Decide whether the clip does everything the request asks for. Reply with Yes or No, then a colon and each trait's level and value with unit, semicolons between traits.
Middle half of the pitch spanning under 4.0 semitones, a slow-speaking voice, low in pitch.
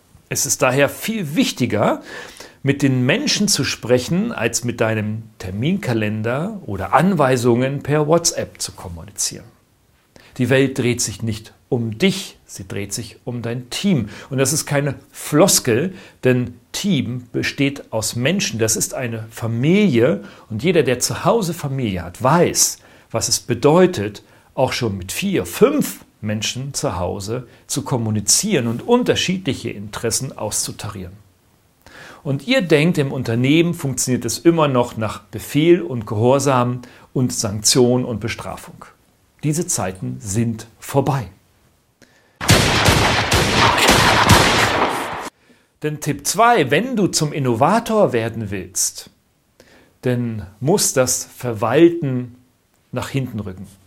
No: average, 4.7 semitones; slow, 120 wpm; low, 125 Hz